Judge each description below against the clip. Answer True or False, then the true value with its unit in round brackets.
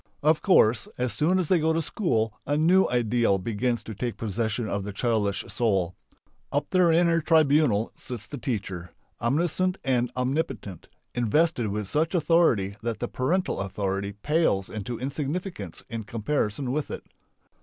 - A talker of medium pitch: False (120 Hz)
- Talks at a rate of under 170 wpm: True (155 wpm)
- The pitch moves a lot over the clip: True (6.8 semitones)